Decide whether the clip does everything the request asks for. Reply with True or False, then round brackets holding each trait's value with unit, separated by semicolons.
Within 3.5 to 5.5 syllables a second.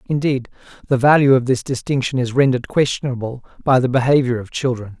False (6.2 syllables/s)